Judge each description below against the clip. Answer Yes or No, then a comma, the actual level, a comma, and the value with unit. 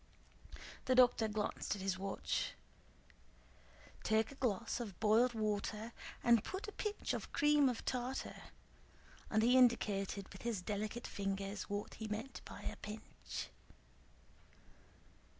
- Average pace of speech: No, slow, 130 wpm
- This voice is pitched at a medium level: No, high, 220 Hz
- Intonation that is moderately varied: Yes, average, 3.3 semitones